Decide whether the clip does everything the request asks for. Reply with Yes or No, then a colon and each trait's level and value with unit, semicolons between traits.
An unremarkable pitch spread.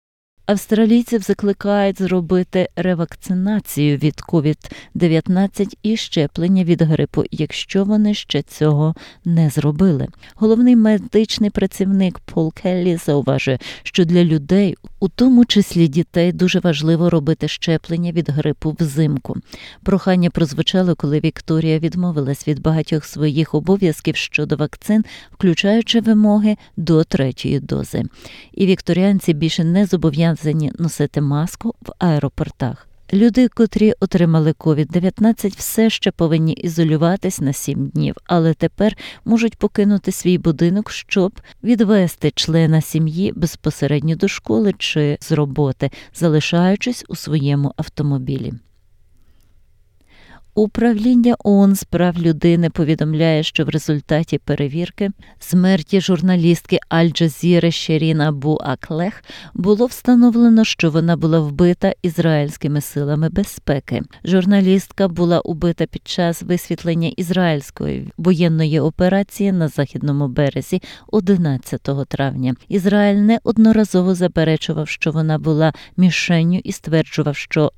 Yes: average, 4.1 semitones